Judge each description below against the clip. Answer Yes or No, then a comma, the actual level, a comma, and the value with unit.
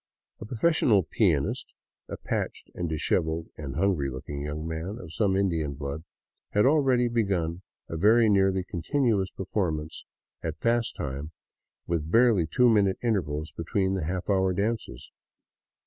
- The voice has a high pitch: No, very low, 95 Hz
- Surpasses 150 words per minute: No, average, 145 wpm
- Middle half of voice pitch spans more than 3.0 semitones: Yes, average, 5.3 semitones